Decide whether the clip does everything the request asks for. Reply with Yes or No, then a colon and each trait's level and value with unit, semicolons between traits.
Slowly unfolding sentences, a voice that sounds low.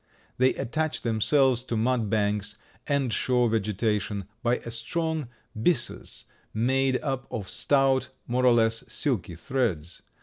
Yes: slow, 130 wpm; low, 120 Hz